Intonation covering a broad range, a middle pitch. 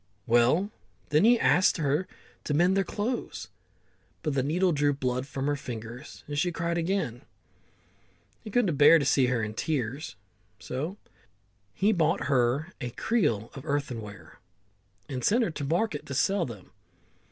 Yes: wide, 5.8 semitones; medium, 145 Hz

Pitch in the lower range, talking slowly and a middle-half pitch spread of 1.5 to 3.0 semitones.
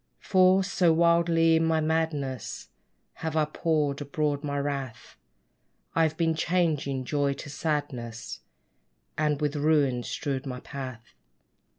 No: medium, 150 Hz; slow, 120 wpm; average, 2.7 semitones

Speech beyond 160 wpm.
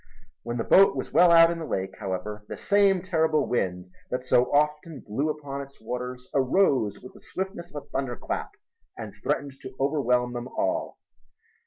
Yes: average, 175 wpm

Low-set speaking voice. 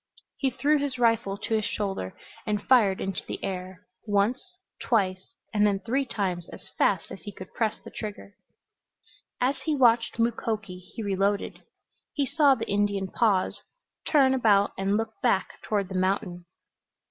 No: high, 205 Hz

